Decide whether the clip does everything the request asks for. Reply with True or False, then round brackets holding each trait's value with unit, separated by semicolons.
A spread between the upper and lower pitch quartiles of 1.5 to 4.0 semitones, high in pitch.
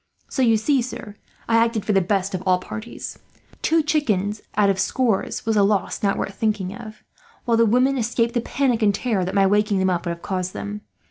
True (3.3 semitones; 210 Hz)